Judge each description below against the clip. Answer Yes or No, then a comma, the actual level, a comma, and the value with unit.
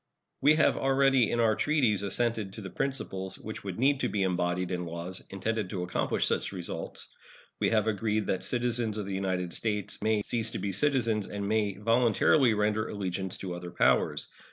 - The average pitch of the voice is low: Yes, low, 105 Hz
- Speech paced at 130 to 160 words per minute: No, average, 185 wpm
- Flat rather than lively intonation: No, average, 3.5 semitones